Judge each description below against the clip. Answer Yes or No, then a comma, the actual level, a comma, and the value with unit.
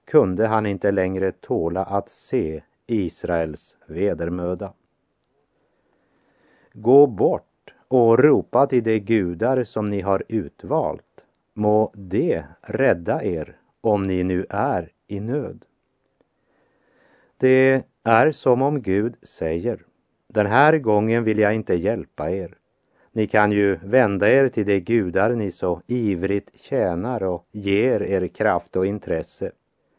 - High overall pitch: No, low, 105 Hz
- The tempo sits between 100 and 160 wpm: Yes, average, 125 wpm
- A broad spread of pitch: No, average, 3.4 semitones